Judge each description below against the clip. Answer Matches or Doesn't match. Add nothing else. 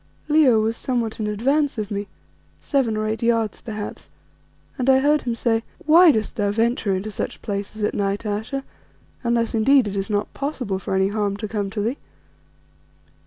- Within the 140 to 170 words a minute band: Doesn't match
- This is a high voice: Matches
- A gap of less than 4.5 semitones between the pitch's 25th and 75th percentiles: Matches